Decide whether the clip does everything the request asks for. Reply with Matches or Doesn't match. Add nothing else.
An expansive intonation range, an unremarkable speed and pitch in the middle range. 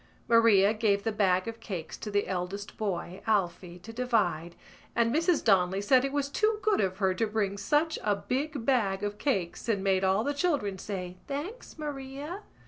Doesn't match